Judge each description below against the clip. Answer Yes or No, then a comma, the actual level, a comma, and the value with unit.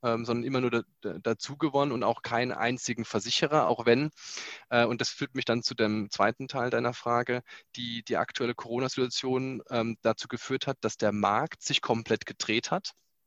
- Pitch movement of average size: No, narrow, 2.1 semitones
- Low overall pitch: Yes, low, 120 Hz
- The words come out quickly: No, average, 165 wpm